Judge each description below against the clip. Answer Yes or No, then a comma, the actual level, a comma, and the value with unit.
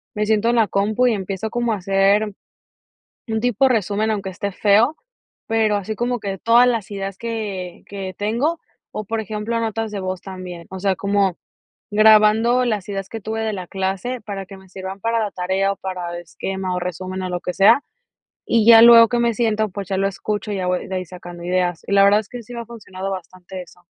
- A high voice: Yes, high, 200 Hz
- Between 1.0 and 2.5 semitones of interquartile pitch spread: No, average, 2.9 semitones